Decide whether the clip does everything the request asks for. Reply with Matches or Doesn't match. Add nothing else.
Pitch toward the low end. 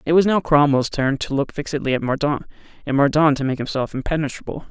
Doesn't match